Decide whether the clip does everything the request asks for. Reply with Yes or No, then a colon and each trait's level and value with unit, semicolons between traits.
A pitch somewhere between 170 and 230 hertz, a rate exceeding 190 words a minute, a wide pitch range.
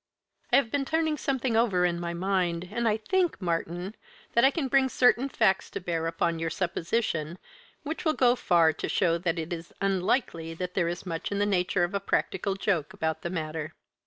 Yes: medium, 185 Hz; fast, 205 wpm; wide, 5.7 semitones